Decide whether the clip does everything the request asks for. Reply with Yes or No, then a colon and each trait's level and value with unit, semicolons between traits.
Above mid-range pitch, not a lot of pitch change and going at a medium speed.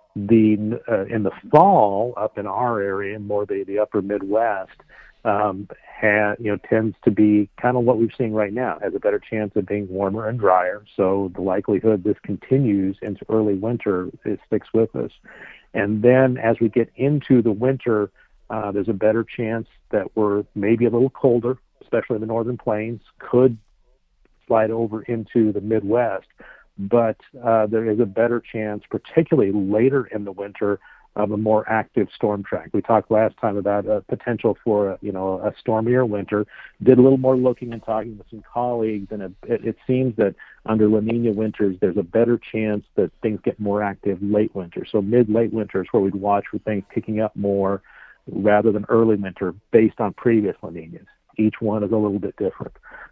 No: low, 110 Hz; narrow, 2.1 semitones; average, 190 wpm